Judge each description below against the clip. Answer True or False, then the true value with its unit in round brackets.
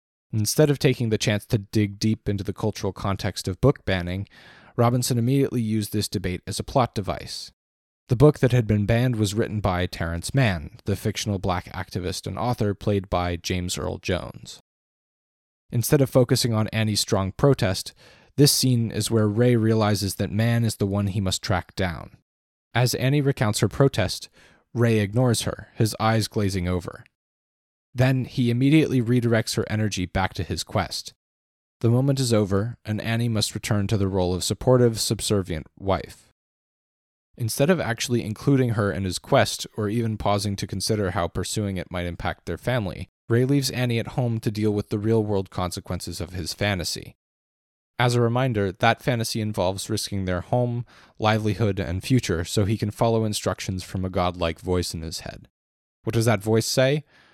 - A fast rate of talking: False (175 wpm)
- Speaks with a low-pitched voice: True (105 Hz)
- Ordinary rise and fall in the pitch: True (4.1 semitones)